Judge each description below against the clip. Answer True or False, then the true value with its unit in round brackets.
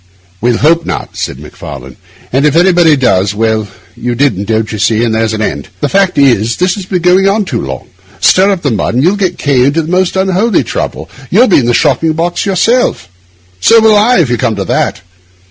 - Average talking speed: False (215 wpm)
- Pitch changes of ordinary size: False (8.7 semitones)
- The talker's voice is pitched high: False (145 Hz)